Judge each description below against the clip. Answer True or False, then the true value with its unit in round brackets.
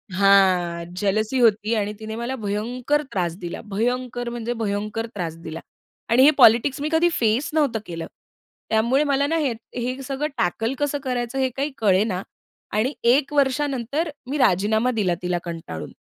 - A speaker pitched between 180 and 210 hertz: False (230 Hz)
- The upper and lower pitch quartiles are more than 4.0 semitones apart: True (4.9 semitones)